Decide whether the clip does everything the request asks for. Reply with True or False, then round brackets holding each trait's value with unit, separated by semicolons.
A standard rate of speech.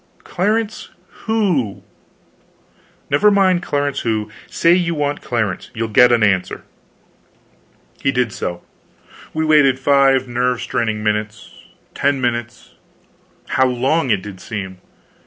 False (120 wpm)